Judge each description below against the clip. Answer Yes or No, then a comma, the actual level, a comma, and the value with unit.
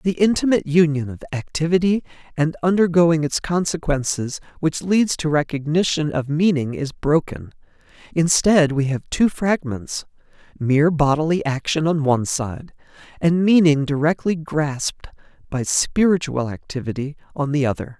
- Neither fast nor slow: No, slow, 125 wpm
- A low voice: No, medium, 155 Hz